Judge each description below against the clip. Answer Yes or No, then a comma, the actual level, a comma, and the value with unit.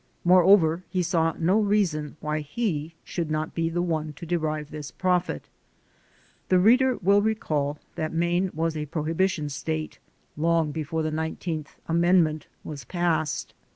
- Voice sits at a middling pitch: Yes, medium, 165 Hz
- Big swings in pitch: No, average, 2.7 semitones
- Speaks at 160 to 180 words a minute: No, average, 150 wpm